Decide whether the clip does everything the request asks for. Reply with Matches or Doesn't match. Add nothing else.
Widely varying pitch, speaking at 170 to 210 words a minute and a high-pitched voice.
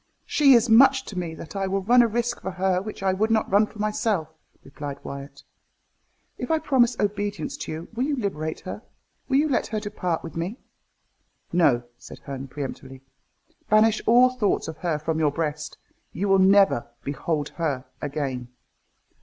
Matches